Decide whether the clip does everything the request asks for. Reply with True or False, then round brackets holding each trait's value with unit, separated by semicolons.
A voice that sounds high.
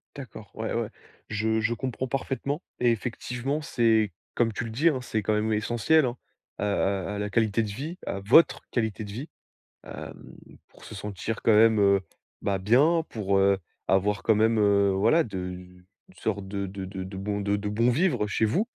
False (110 Hz)